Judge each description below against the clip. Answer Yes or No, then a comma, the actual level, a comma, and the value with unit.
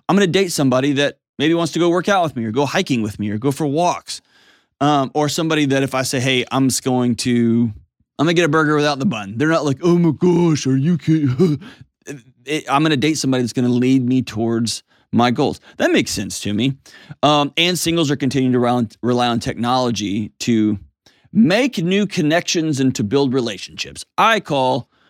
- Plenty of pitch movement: No, average, 4.6 semitones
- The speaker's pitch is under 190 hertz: Yes, medium, 140 Hz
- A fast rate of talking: Yes, fast, 215 wpm